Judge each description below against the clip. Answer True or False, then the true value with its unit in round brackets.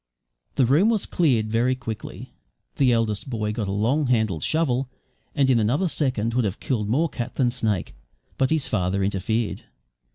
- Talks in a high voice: False (120 Hz)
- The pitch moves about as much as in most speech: True (4.0 semitones)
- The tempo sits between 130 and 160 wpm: False (170 wpm)